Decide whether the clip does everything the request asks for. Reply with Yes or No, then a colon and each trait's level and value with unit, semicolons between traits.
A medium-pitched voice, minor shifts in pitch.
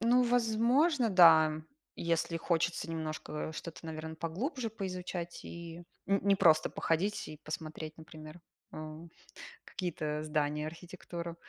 No: medium, 170 Hz; average, 3.9 semitones